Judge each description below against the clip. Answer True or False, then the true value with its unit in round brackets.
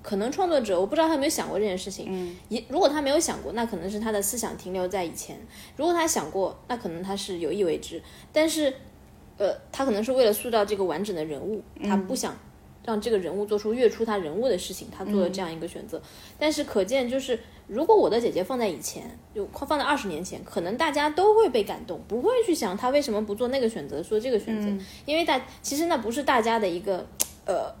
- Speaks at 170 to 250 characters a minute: False (355 characters per minute)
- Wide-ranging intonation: True (6.9 semitones)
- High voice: True (225 Hz)